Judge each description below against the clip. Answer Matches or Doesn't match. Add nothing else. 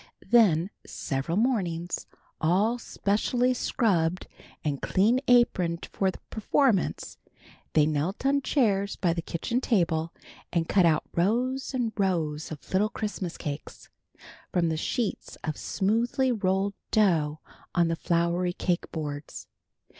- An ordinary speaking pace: Doesn't match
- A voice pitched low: Doesn't match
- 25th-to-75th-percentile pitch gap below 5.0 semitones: Doesn't match